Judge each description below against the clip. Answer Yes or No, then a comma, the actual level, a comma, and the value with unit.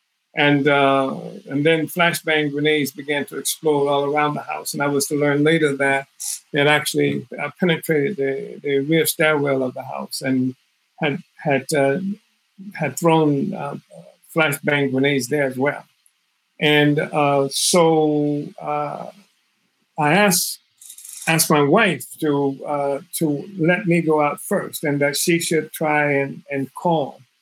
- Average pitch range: No, narrow, 2.1 semitones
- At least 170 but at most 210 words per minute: No, average, 145 wpm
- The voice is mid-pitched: Yes, medium, 150 Hz